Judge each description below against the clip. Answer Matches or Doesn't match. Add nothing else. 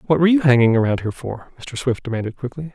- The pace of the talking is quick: Matches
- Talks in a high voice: Doesn't match